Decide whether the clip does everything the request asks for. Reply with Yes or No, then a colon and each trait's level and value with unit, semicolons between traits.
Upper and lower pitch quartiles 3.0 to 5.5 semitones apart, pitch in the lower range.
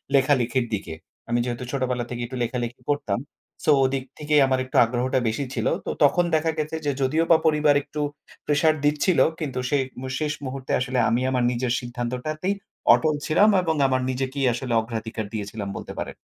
Yes: average, 3.6 semitones; low, 130 Hz